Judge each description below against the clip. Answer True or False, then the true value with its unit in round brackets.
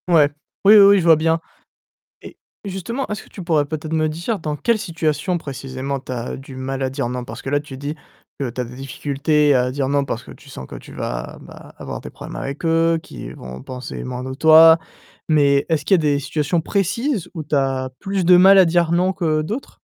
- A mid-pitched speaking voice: True (155 Hz)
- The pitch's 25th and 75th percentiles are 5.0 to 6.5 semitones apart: False (4.2 semitones)